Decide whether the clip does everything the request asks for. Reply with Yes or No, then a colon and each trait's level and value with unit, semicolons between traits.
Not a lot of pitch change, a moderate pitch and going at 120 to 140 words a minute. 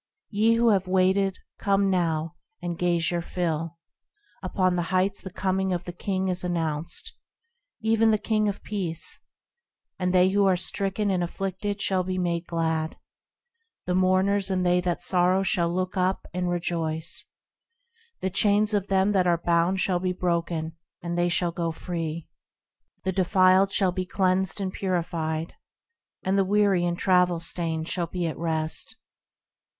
No: narrow, 2.0 semitones; medium, 180 Hz; average, 160 wpm